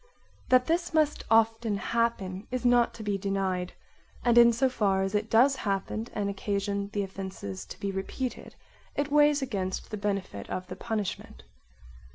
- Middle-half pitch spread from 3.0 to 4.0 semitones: Yes, average, 3.6 semitones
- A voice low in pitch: No, high, 210 Hz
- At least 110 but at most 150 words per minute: No, average, 165 wpm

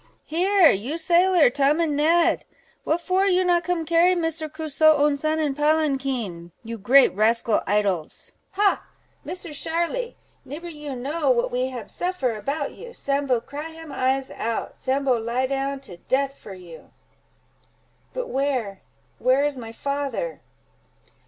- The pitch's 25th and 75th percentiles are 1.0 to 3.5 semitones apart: No, average, 4.7 semitones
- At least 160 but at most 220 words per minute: No, average, 140 wpm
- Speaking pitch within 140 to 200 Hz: No, very high, 280 Hz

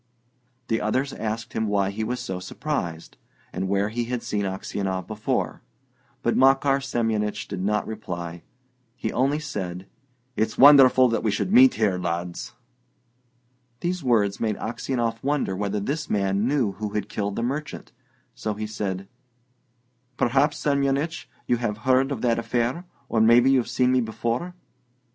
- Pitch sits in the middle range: No, low, 115 Hz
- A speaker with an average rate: Yes, average, 155 wpm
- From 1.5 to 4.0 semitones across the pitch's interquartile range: No, average, 4.5 semitones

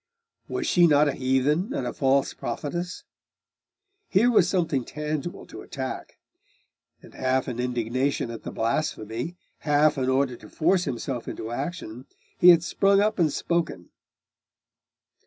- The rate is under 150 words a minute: Yes, average, 140 wpm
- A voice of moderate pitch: Yes, medium, 145 Hz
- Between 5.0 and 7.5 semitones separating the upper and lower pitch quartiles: Yes, average, 5.3 semitones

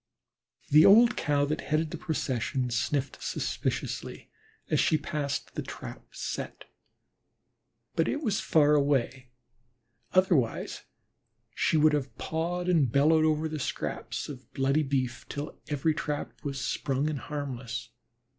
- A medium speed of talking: No, slow, 130 wpm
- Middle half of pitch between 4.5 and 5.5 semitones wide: No, average, 2.8 semitones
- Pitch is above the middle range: No, medium, 145 Hz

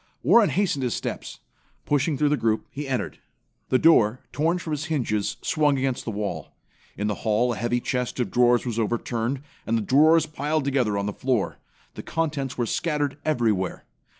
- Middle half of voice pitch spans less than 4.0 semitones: No, average, 4.5 semitones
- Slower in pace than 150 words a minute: No, average, 180 wpm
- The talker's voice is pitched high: No, low, 130 Hz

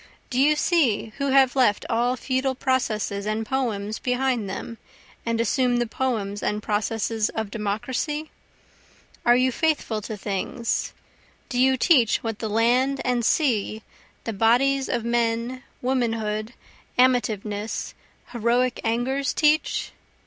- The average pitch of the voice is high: Yes, high, 240 Hz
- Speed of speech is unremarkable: No, slow, 125 wpm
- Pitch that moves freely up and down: No, average, 3.1 semitones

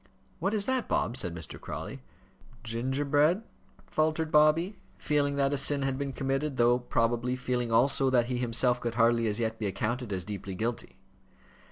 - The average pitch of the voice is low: Yes, low, 125 Hz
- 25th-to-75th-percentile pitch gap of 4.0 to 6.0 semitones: No, average, 3.6 semitones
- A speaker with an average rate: Yes, average, 170 wpm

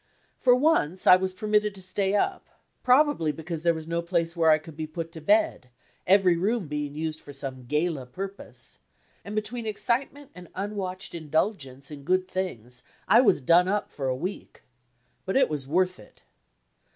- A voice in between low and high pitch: Yes, medium, 180 Hz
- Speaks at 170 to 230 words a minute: Yes, average, 175 wpm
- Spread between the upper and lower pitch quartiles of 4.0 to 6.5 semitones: Yes, average, 4.8 semitones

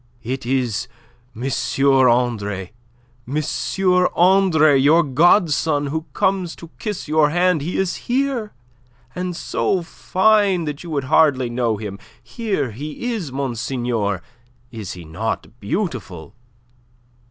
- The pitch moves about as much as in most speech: No, wide, 7.0 semitones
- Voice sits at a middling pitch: Yes, medium, 150 Hz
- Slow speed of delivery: Yes, slow, 120 wpm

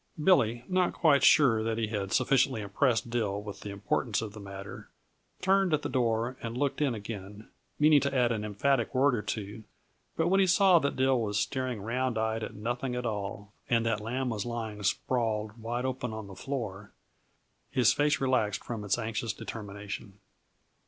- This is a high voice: No, low, 115 Hz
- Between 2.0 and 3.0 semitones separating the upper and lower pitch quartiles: No, average, 3.8 semitones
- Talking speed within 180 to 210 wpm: Yes, average, 185 wpm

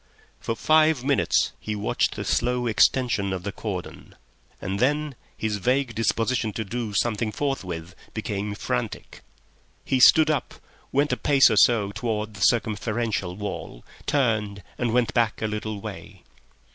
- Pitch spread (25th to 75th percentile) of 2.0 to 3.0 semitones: No, average, 3.5 semitones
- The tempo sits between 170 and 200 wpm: No, average, 145 wpm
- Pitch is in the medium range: No, low, 110 Hz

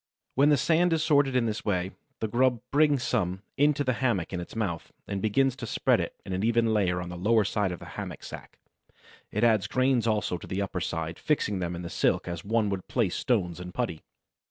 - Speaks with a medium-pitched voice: No, low, 110 Hz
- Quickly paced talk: Yes, fast, 225 wpm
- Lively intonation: Yes, wide, 5.9 semitones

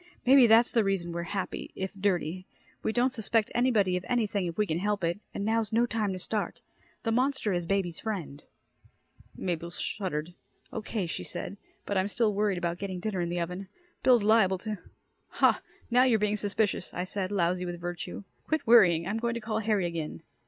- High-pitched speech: Yes, high, 200 Hz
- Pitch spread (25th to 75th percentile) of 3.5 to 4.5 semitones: Yes, average, 3.9 semitones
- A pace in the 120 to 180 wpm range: No, average, 195 wpm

